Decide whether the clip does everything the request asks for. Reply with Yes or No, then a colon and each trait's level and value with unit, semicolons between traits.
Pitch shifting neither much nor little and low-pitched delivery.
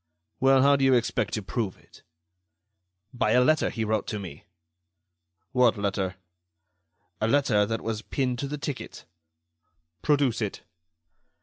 Yes: average, 4.2 semitones; low, 120 Hz